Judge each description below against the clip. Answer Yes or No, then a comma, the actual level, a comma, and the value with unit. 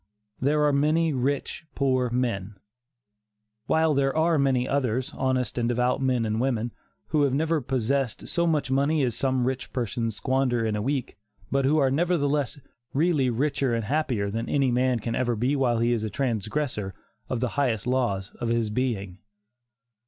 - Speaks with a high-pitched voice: No, low, 130 Hz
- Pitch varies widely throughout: No, average, 3.2 semitones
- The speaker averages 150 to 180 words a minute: Yes, average, 175 wpm